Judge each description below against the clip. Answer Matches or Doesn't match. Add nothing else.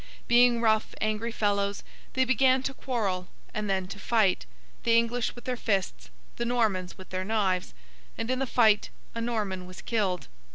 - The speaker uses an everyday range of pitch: Matches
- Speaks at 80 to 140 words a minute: Doesn't match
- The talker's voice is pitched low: Doesn't match